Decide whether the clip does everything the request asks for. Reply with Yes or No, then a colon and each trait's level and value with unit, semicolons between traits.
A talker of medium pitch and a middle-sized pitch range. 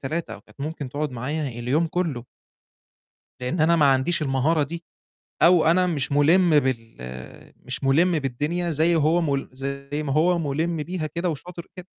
Yes: medium, 155 Hz; average, 3.6 semitones